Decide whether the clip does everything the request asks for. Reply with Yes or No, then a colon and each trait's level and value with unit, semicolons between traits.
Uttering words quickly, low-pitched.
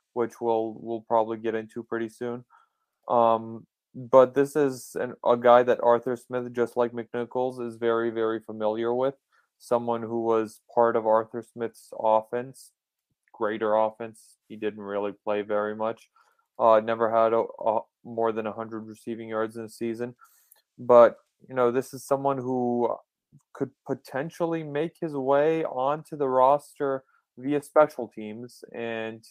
No: average, 150 wpm; low, 120 Hz